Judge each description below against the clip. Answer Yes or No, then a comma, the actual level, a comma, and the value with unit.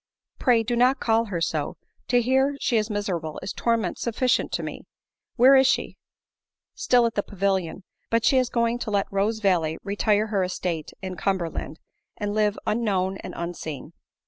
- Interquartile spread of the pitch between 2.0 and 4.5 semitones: Yes, average, 4.2 semitones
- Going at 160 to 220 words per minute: Yes, average, 190 wpm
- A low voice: No, high, 205 Hz